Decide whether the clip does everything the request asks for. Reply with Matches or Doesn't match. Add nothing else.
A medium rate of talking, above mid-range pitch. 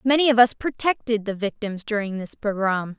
Matches